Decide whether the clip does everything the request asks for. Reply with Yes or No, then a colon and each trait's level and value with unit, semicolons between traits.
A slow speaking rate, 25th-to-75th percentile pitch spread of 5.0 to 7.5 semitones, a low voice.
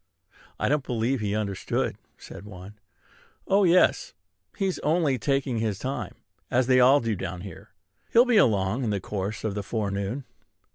No: average, 160 wpm; average, 5.3 semitones; low, 115 Hz